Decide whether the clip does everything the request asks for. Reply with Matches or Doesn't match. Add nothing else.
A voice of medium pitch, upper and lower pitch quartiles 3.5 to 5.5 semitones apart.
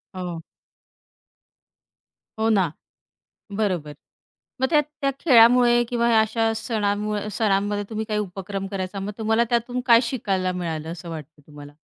Doesn't match